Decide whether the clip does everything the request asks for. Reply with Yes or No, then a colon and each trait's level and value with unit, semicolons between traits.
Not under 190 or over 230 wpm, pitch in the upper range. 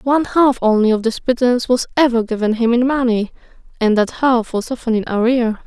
Yes: average, 200 wpm; high, 240 Hz